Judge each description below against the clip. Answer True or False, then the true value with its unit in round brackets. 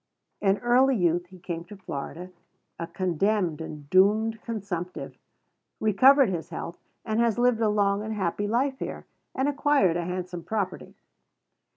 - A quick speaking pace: False (150 wpm)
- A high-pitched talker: True (200 Hz)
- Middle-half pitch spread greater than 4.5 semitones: False (4.2 semitones)